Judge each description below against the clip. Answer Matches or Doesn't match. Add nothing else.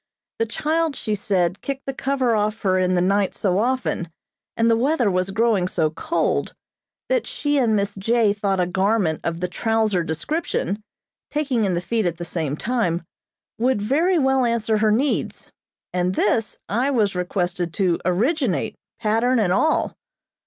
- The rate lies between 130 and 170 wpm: Matches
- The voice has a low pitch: Doesn't match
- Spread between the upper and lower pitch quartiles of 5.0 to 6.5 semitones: Matches